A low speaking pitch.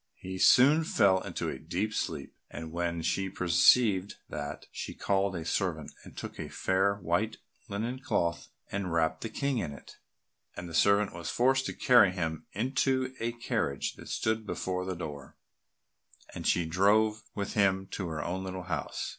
Yes: very low, 95 Hz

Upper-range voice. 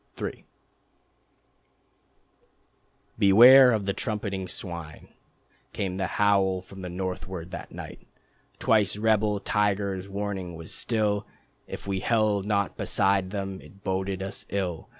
No: low, 100 Hz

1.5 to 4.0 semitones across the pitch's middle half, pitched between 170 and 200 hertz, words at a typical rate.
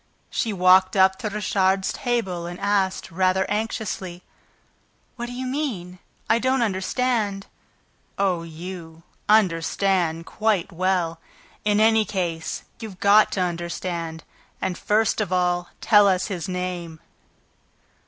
No: average, 3.0 semitones; high, 190 Hz; slow, 125 wpm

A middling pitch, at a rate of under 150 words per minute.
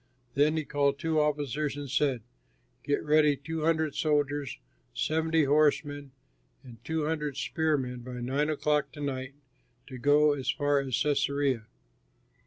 Yes: medium, 145 Hz; average, 140 wpm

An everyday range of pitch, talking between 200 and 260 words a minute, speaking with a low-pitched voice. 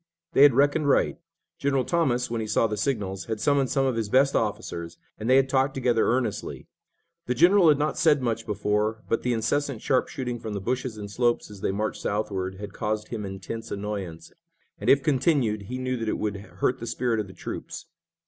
Yes: average, 4.0 semitones; fast, 205 wpm; low, 115 Hz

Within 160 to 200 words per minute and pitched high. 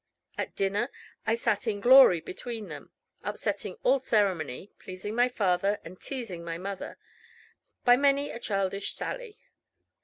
No: average, 140 wpm; high, 210 Hz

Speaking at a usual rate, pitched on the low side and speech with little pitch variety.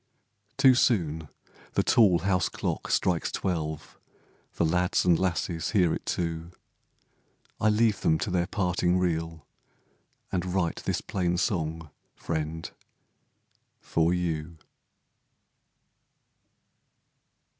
No: slow, 100 wpm; very low, 85 Hz; narrow, 2.3 semitones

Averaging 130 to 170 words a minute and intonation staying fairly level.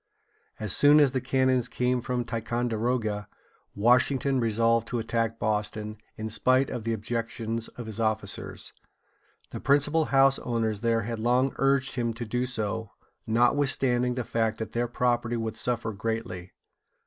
Yes: average, 150 wpm; narrow, 2.1 semitones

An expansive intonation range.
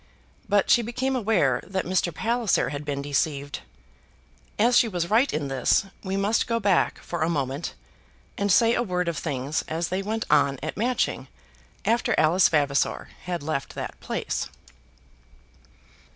Yes: wide, 7.1 semitones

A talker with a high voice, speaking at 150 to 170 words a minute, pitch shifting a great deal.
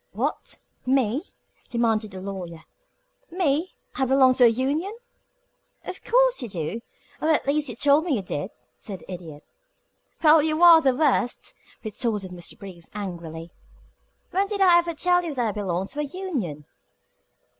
Yes: very high, 255 Hz; average, 160 wpm; wide, 8.6 semitones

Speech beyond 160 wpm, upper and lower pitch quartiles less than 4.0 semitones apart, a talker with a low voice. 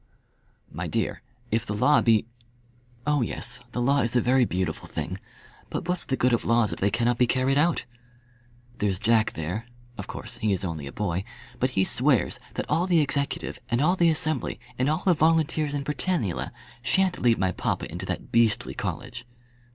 No: average, 190 wpm; wide, 5.4 semitones; low, 120 Hz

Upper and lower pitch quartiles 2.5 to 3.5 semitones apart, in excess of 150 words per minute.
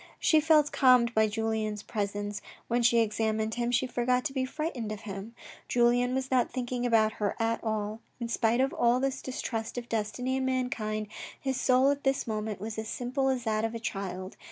Yes: average, 2.8 semitones; average, 200 wpm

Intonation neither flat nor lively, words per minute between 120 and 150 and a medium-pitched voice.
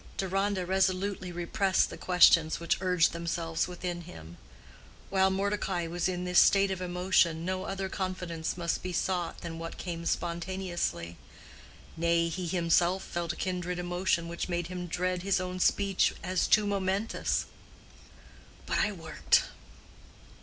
No: narrow, 2.0 semitones; average, 140 wpm; medium, 180 Hz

